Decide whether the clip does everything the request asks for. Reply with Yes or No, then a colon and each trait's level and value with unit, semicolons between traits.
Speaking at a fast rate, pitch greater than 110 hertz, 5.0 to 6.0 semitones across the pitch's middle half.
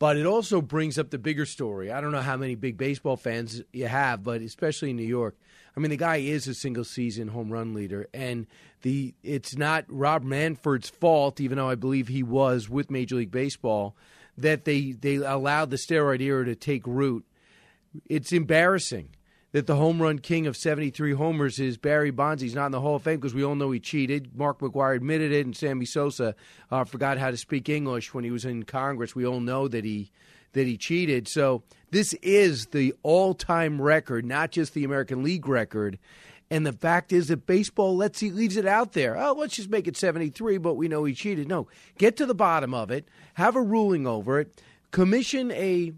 No: fast, 215 wpm; medium, 140 Hz; average, 3.8 semitones